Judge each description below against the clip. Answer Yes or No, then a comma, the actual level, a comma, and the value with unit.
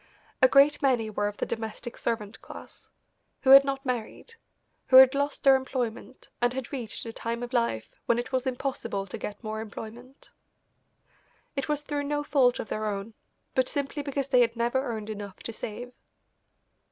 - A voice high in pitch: Yes, high, 245 Hz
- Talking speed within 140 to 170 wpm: No, average, 180 wpm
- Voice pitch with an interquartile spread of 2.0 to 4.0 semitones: Yes, average, 3.5 semitones